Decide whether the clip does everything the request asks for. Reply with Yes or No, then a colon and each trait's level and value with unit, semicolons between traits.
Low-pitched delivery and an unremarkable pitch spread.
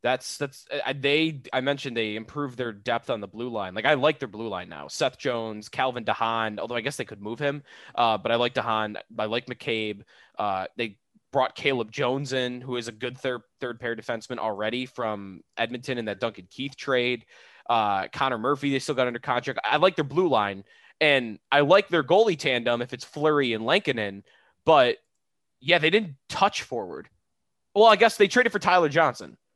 Yes: low, 125 Hz; average, 4.3 semitones